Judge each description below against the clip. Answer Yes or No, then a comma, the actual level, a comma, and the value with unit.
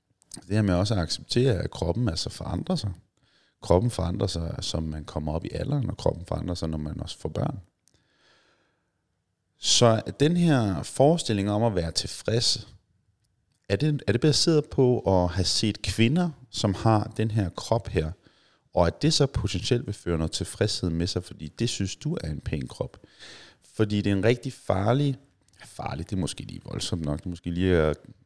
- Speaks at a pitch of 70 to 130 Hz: Yes, low, 105 Hz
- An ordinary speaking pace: Yes, average, 190 wpm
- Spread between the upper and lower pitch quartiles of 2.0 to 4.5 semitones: No, average, 5.3 semitones